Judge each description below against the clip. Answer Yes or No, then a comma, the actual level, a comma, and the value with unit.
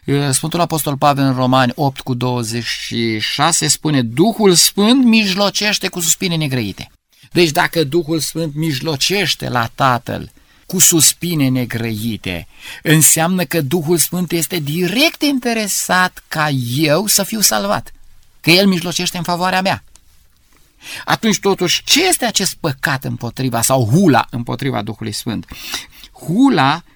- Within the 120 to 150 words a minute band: Yes, average, 125 wpm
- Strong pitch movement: Yes, wide, 6.2 semitones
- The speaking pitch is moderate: Yes, medium, 155 Hz